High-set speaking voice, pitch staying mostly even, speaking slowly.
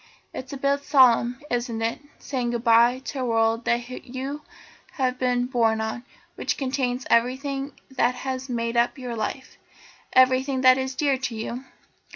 No: very high, 255 Hz; narrow, 1.8 semitones; average, 165 wpm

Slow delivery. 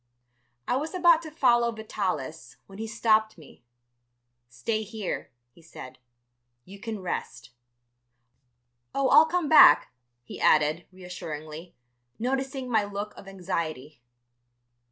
Yes: slow, 115 wpm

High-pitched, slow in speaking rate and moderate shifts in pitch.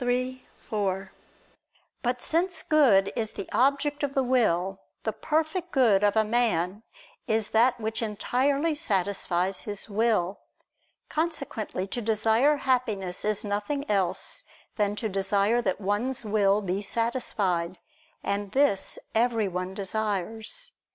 Yes: high, 220 Hz; slow, 125 wpm; average, 4.3 semitones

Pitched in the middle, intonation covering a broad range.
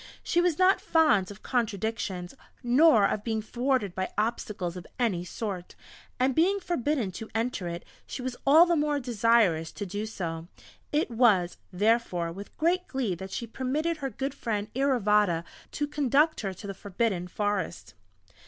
No: high, 225 Hz; wide, 6.1 semitones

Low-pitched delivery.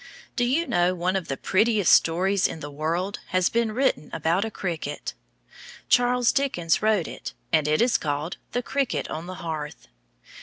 No: medium, 185 Hz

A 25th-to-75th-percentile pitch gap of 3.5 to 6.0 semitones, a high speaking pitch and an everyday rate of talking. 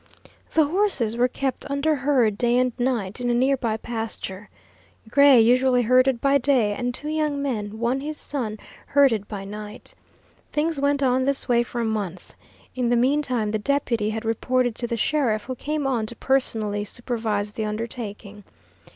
Yes: average, 3.9 semitones; high, 245 Hz; average, 175 wpm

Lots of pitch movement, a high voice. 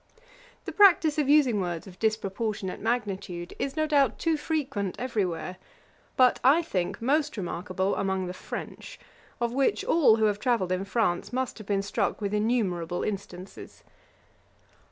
Yes: wide, 5.8 semitones; high, 215 Hz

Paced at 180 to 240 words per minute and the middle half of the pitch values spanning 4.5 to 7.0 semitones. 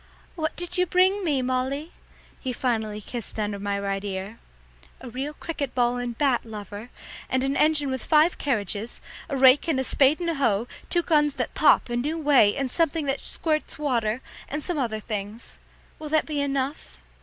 Yes: average, 190 wpm; average, 5.1 semitones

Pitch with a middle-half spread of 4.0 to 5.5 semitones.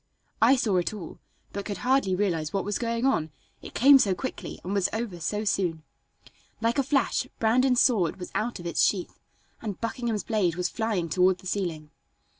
Yes: average, 4.5 semitones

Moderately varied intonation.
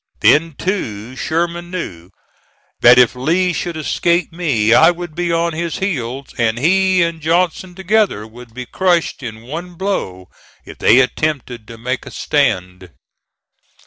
No: wide, 6.6 semitones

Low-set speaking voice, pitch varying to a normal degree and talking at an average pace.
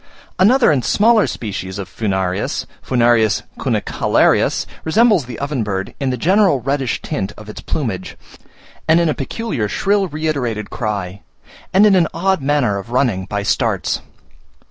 No: low, 130 Hz; wide, 8.3 semitones; average, 145 wpm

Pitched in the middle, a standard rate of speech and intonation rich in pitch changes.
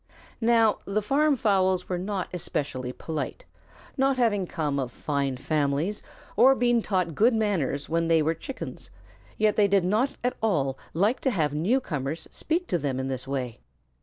Yes: medium, 180 Hz; average, 165 wpm; wide, 7.3 semitones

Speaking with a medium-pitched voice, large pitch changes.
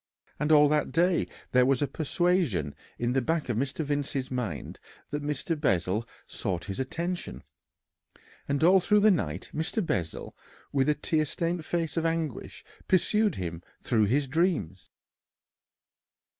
Yes: medium, 145 Hz; wide, 5.7 semitones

